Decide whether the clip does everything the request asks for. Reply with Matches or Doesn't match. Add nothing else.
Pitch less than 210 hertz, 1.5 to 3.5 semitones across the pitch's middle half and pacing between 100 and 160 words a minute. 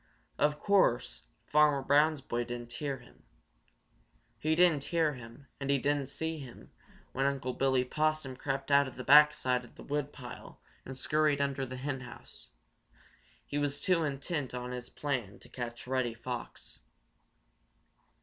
Matches